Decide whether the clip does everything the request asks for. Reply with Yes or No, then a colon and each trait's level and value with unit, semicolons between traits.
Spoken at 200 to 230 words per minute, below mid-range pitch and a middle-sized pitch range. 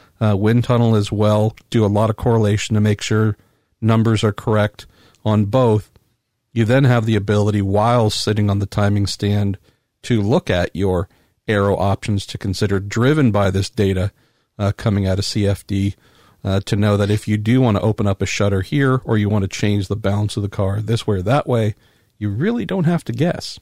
No: fast, 205 wpm; low, 105 Hz; narrow, 2.3 semitones